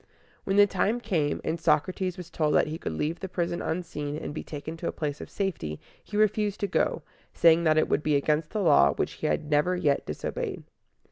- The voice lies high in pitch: No, medium, 160 Hz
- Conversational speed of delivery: No, fast, 220 wpm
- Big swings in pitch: No, average, 3.6 semitones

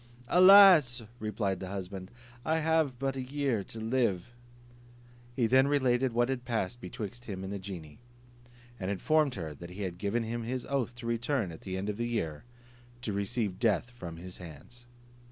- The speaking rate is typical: Yes, average, 180 wpm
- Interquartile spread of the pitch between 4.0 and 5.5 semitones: Yes, average, 5.0 semitones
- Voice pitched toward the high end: No, low, 115 Hz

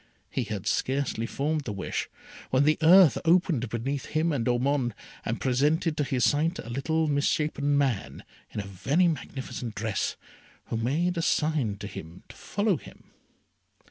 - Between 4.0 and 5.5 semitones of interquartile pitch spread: Yes, average, 5.0 semitones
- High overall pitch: No, medium, 140 Hz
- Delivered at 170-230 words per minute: No, average, 160 wpm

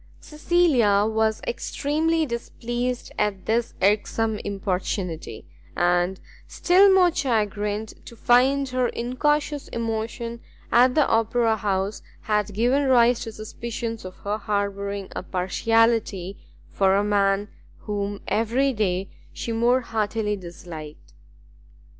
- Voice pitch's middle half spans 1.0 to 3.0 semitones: No, average, 3.4 semitones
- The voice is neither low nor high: No, high, 220 Hz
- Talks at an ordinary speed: No, slow, 110 wpm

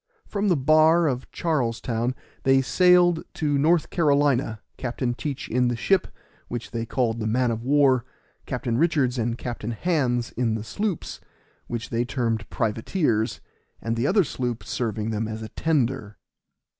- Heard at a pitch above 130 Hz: No, low, 125 Hz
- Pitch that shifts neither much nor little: Yes, average, 4.6 semitones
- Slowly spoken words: No, average, 155 wpm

